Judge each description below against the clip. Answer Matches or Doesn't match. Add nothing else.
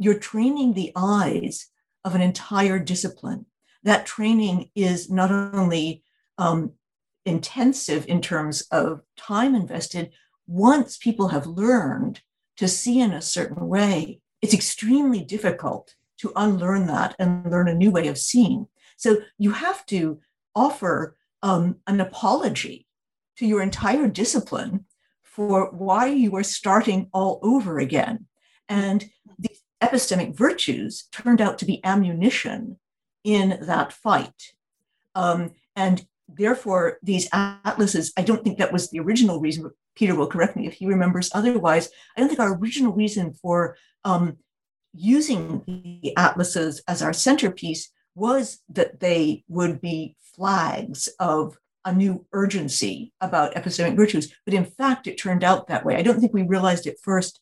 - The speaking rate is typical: Matches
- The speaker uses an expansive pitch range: Doesn't match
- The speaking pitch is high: Matches